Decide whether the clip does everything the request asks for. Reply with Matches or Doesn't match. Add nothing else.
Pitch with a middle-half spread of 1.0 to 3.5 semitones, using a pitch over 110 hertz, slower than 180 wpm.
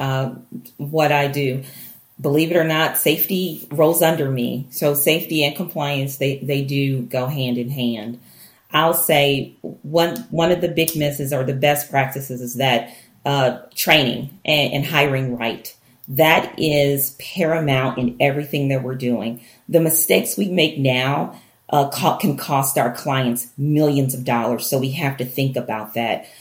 Matches